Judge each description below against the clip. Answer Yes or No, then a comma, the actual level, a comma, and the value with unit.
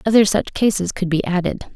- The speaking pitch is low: No, high, 195 Hz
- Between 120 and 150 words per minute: No, fast, 205 wpm